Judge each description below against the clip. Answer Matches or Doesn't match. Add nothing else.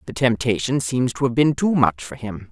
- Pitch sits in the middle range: Doesn't match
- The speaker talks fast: Matches